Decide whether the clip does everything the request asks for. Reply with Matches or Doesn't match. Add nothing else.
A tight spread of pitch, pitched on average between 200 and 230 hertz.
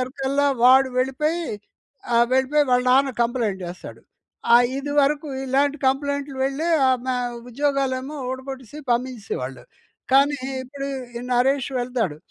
Doesn't match